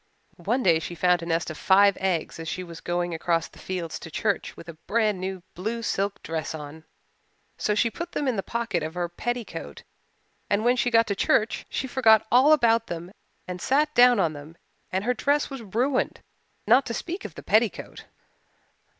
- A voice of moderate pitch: No, high, 200 Hz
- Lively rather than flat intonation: Yes, wide, 6.0 semitones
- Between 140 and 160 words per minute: No, average, 200 wpm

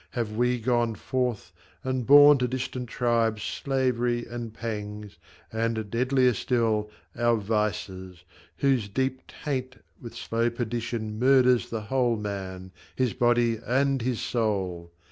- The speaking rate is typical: No, slow, 125 wpm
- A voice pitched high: No, low, 120 Hz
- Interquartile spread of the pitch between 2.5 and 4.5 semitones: Yes, average, 2.9 semitones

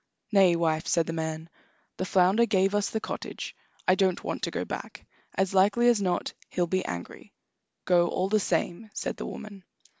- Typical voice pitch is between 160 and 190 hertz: Yes, medium, 185 Hz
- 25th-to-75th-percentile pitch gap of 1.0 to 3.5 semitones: Yes, average, 2.8 semitones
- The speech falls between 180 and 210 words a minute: Yes, average, 185 wpm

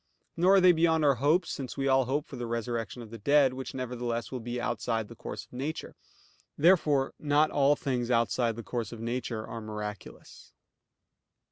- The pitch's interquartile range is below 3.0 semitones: No, average, 3.7 semitones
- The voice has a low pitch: Yes, low, 125 Hz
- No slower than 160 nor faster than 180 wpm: No, average, 195 wpm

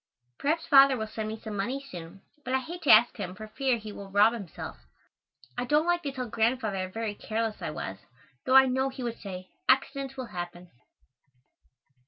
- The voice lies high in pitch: Yes, high, 230 Hz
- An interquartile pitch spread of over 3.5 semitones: Yes, average, 4.5 semitones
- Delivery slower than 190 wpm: No, average, 200 wpm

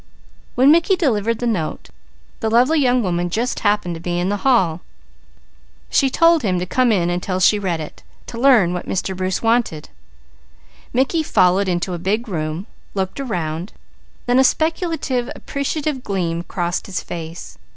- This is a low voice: No, high, 205 Hz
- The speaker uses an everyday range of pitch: No, wide, 6.2 semitones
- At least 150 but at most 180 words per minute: Yes, average, 160 wpm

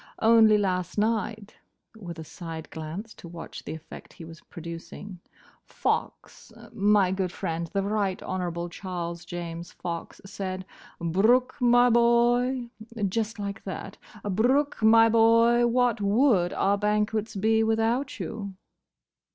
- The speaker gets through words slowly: Yes, slow, 115 wpm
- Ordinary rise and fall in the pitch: Yes, average, 4.3 semitones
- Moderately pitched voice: No, high, 205 Hz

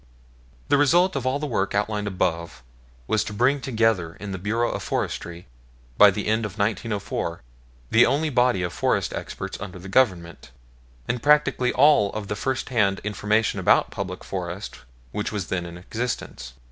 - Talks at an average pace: Yes, average, 170 wpm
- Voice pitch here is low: Yes, low, 105 Hz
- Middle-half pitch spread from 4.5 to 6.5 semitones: Yes, average, 5.0 semitones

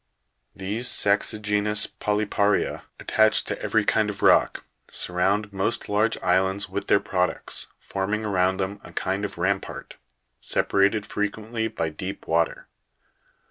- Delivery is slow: Yes, slow, 130 wpm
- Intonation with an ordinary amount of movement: No, narrow, 1.8 semitones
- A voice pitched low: Yes, low, 100 Hz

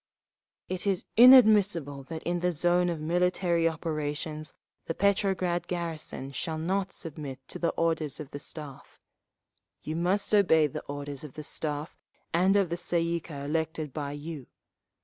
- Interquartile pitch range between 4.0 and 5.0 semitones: No, average, 2.8 semitones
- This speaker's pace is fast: No, average, 155 wpm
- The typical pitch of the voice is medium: Yes, medium, 165 Hz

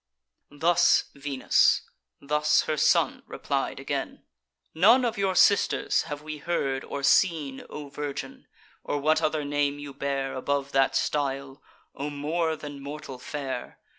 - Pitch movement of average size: No, narrow, 2.0 semitones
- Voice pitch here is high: No, medium, 145 Hz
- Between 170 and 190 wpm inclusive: No, slow, 135 wpm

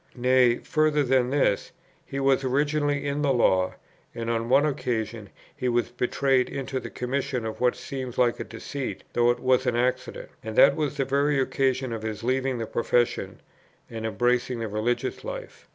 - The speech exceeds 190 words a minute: No, average, 180 wpm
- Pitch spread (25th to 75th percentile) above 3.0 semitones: No, narrow, 2.5 semitones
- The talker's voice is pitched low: Yes, low, 125 Hz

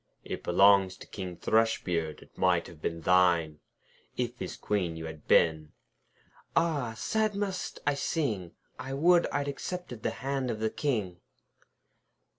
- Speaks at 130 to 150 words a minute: Yes, average, 145 wpm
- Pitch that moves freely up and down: Yes, wide, 8.4 semitones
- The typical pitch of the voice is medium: No, low, 105 Hz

